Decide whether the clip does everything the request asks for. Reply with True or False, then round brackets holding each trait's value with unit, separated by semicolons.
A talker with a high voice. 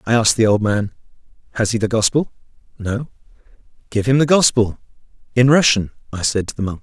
False (115 Hz)